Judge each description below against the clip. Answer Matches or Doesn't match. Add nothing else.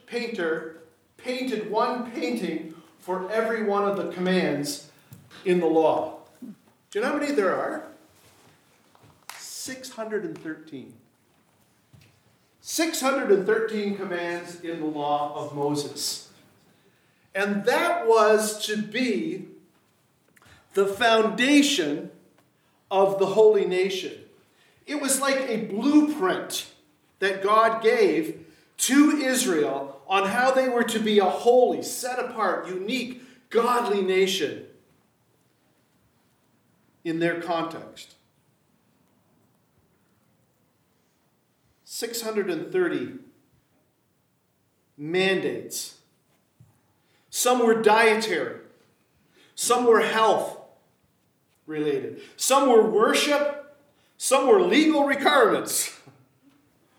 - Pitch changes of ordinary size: Doesn't match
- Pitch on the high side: Matches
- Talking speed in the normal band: Doesn't match